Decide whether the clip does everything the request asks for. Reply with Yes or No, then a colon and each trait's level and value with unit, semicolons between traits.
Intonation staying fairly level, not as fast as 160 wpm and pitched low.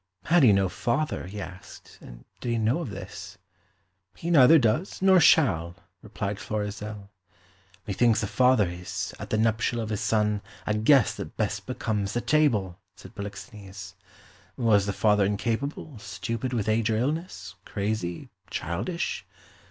No: average, 3.7 semitones; average, 150 wpm; low, 110 Hz